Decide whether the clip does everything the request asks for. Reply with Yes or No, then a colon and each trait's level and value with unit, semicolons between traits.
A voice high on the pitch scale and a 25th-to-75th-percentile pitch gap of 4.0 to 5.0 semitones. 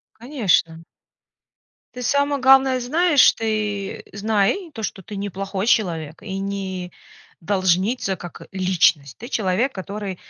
Yes: high, 200 Hz; average, 4.3 semitones